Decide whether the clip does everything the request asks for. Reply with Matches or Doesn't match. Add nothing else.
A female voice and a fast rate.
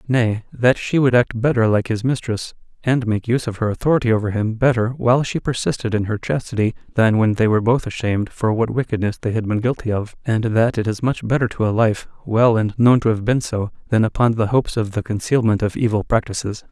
Doesn't match